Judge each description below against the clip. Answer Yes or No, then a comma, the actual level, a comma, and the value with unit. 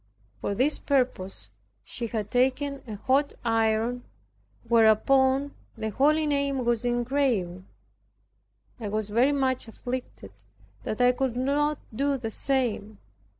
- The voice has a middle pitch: No, high, 245 Hz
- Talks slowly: Yes, slow, 120 wpm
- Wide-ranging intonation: No, average, 3.8 semitones